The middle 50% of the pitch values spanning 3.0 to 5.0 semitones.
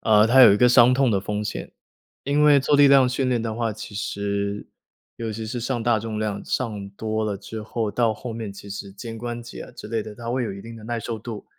No: narrow, 2.4 semitones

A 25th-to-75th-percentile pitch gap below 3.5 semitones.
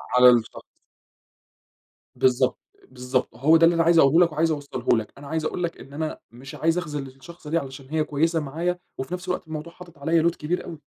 No: average, 3.8 semitones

